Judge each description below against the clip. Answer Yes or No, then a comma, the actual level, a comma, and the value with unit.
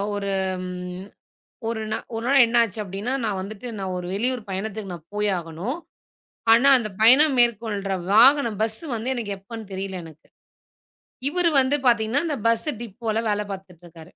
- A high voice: Yes, high, 220 Hz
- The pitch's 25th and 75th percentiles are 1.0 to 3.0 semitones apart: No, average, 3.7 semitones